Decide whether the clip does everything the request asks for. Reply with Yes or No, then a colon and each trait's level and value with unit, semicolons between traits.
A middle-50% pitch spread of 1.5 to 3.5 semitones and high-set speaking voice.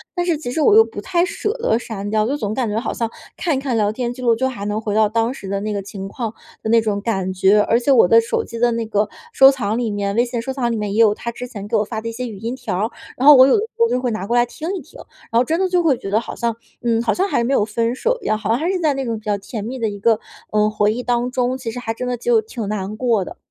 Yes: average, 3.1 semitones; high, 230 Hz